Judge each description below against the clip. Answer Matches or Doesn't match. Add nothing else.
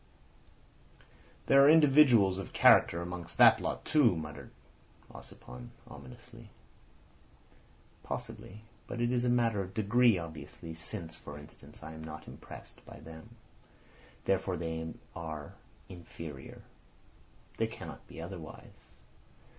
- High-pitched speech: Doesn't match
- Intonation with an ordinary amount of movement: Doesn't match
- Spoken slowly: Matches